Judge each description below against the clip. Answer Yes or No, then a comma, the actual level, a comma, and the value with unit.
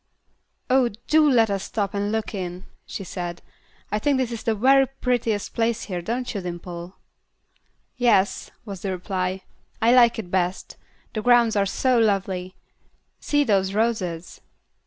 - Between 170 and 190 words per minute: No, average, 155 wpm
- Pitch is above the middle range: Yes, high, 210 Hz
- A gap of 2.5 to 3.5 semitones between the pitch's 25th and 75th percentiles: No, average, 4.2 semitones